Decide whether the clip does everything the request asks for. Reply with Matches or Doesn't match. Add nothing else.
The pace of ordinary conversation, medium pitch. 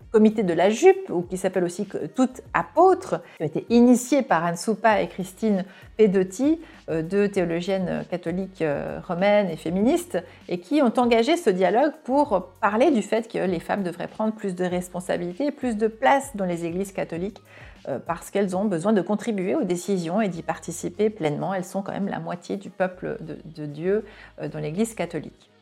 Doesn't match